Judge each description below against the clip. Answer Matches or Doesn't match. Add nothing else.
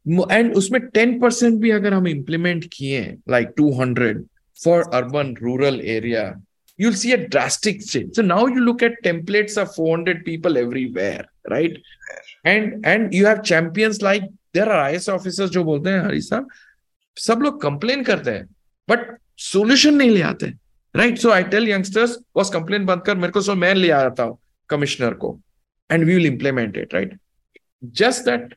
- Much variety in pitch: Matches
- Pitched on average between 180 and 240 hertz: Matches